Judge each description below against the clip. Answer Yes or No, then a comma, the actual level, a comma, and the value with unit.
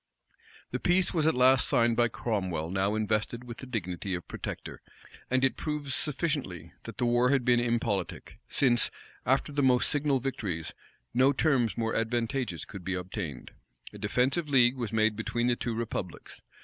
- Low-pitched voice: Yes, low, 120 Hz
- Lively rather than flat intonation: No, average, 4.1 semitones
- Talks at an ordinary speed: Yes, average, 170 wpm